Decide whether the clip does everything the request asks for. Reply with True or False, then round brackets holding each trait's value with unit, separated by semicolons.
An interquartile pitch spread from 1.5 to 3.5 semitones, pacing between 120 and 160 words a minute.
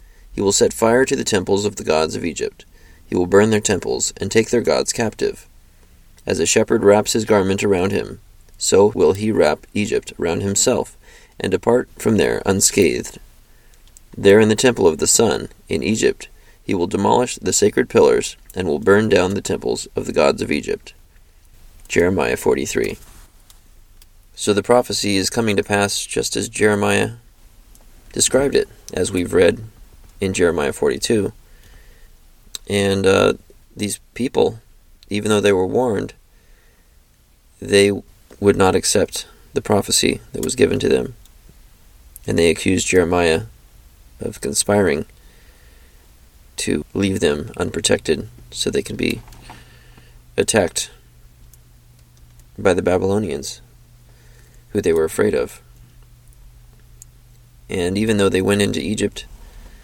False (4.9 semitones; 140 wpm)